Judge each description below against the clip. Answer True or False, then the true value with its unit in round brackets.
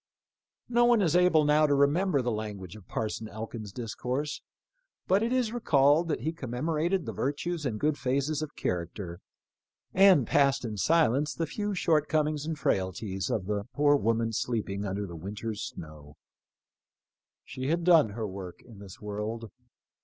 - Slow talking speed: False (160 wpm)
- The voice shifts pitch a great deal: True (6.8 semitones)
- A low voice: True (130 Hz)